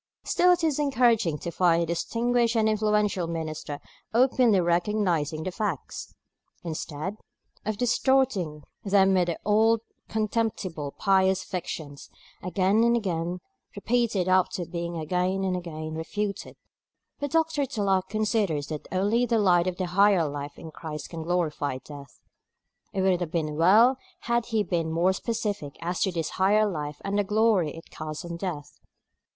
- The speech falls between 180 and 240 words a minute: No, average, 150 wpm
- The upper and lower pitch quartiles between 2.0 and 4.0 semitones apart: No, average, 4.6 semitones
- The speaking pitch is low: No, medium, 185 Hz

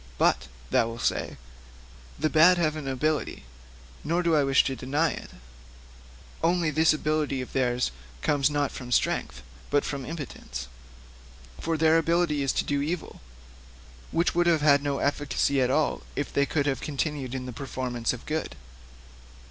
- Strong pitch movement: No, average, 2.9 semitones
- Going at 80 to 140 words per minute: No, average, 165 wpm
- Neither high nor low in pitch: Yes, medium, 145 Hz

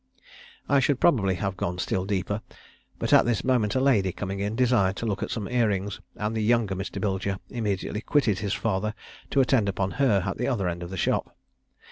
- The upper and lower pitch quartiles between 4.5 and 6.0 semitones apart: No, average, 3.6 semitones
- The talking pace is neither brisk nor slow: No, fast, 210 wpm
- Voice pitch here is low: Yes, low, 105 Hz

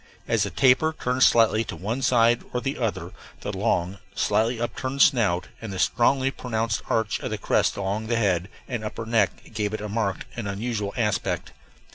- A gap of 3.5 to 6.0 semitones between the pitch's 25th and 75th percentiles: No, average, 3.0 semitones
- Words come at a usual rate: Yes, average, 185 wpm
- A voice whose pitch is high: No, low, 115 Hz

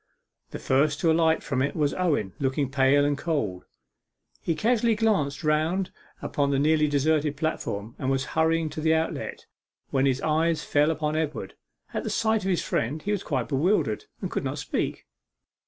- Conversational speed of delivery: Yes, average, 175 wpm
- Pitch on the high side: No, medium, 150 Hz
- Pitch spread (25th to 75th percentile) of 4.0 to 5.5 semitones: No, average, 2.8 semitones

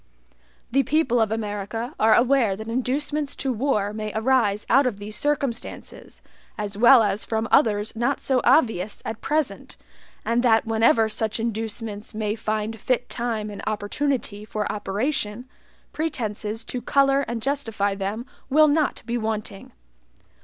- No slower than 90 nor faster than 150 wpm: Yes, average, 145 wpm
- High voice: Yes, high, 225 Hz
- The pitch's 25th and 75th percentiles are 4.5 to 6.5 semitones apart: No, average, 3.4 semitones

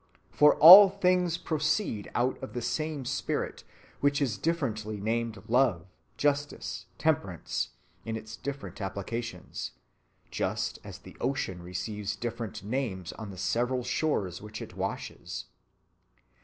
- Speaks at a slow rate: Yes, slow, 125 wpm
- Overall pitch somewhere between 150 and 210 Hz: No, low, 120 Hz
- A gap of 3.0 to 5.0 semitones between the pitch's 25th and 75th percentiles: No, wide, 5.5 semitones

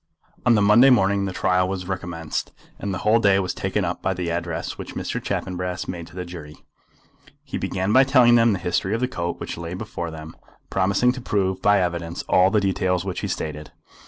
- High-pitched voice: No, very low, 95 Hz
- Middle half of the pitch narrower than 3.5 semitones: Yes, average, 2.8 semitones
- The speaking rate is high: Yes, fast, 215 wpm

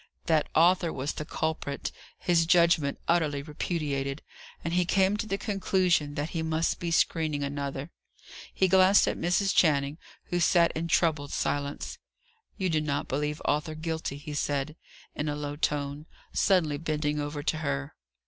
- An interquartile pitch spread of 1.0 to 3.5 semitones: Yes, average, 2.7 semitones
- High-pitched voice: No, medium, 155 Hz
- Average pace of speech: Yes, average, 160 wpm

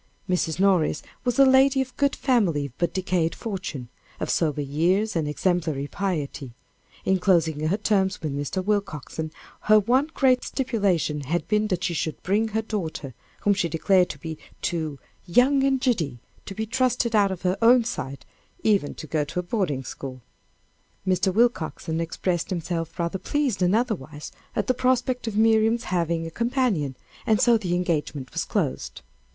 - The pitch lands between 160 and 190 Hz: Yes, medium, 185 Hz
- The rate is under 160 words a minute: No, average, 165 wpm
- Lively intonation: Yes, wide, 5.8 semitones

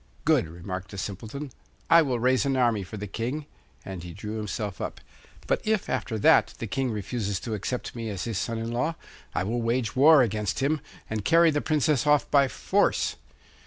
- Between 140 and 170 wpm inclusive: No, average, 200 wpm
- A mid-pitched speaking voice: No, low, 115 Hz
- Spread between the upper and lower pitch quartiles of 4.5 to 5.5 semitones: Yes, average, 4.9 semitones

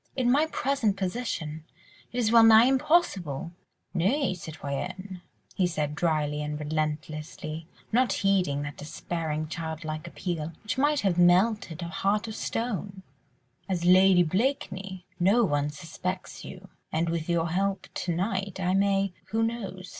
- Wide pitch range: No, average, 4.4 semitones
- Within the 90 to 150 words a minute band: Yes, average, 140 wpm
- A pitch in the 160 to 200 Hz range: Yes, medium, 185 Hz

